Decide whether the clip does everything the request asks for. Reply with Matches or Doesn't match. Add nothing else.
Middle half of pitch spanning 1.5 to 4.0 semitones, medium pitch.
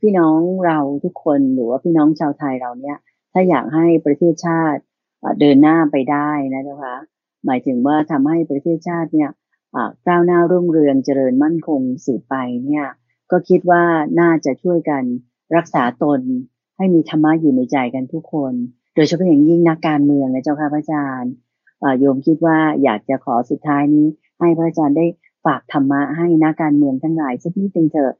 Matches